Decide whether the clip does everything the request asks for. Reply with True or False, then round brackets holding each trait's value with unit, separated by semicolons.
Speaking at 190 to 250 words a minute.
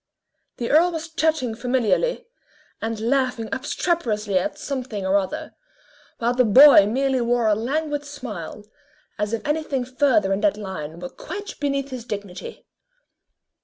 False (140 wpm)